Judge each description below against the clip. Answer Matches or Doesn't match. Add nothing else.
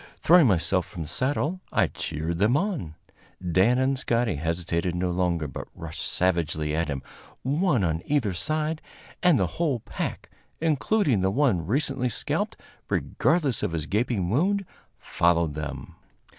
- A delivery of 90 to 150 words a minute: Matches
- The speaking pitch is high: Doesn't match